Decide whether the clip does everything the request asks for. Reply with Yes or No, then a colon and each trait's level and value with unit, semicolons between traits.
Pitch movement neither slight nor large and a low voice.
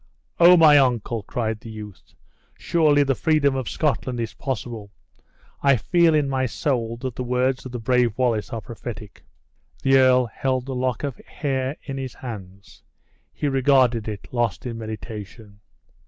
Yes: average, 3.1 semitones; low, 125 Hz